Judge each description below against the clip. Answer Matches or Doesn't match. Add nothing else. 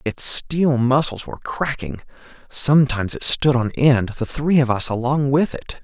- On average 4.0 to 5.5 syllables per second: Matches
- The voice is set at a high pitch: Doesn't match